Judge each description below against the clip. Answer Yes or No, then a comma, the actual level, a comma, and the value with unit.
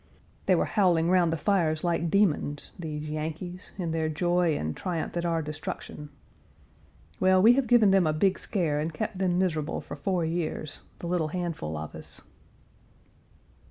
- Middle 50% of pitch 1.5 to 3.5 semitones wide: Yes, average, 3.0 semitones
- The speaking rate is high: No, average, 165 wpm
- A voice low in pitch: No, medium, 170 Hz